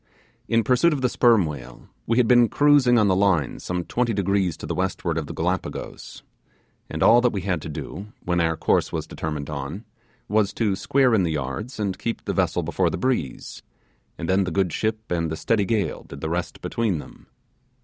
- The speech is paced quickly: Yes, fast, 210 wpm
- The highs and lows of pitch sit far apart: Yes, wide, 5.7 semitones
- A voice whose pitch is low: Yes, very low, 95 Hz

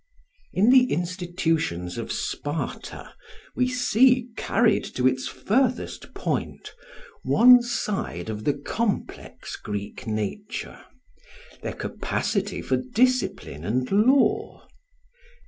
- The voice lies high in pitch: Yes, high, 195 Hz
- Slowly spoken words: Yes, slow, 95 wpm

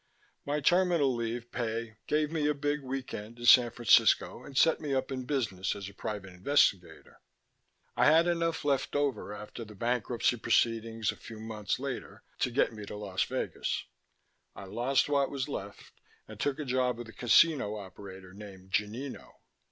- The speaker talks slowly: No, average, 170 wpm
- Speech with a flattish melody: No, average, 5.0 semitones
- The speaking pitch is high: No, low, 120 Hz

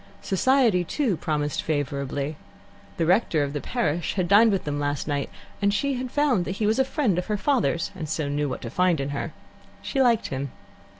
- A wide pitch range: Yes, wide, 7.1 semitones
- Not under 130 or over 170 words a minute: No, average, 200 wpm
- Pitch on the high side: No, medium, 175 Hz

